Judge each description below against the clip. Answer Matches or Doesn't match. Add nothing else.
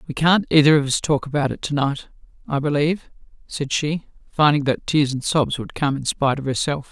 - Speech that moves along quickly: Matches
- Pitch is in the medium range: Matches